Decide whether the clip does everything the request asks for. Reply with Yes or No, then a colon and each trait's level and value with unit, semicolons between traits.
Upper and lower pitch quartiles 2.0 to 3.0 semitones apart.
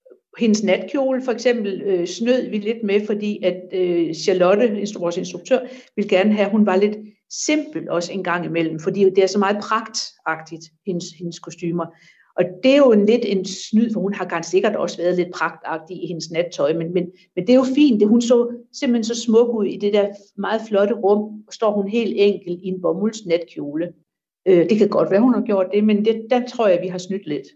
No: average, 3.8 semitones